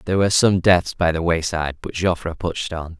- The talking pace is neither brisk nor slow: No, fast, 220 wpm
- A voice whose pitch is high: No, very low, 85 Hz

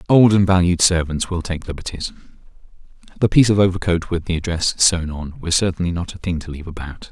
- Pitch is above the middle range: No, very low, 90 Hz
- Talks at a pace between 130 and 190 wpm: No, average, 200 wpm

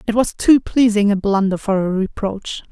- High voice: Yes, high, 205 Hz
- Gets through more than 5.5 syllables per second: No, 4.8 syllables/s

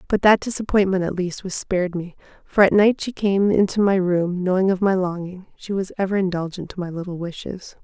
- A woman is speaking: Yes, female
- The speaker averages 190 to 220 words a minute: Yes, fast, 205 wpm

